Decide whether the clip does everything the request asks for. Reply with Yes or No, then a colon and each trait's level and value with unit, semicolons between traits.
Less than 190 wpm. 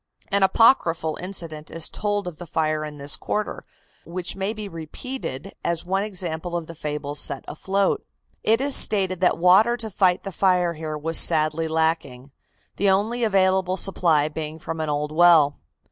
Yes: average, 170 wpm